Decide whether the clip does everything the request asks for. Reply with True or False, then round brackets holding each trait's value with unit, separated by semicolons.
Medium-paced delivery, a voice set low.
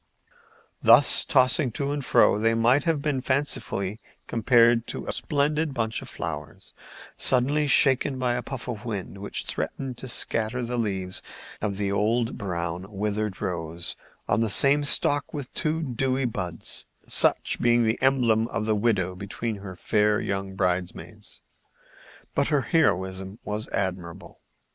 True (150 wpm; 115 Hz)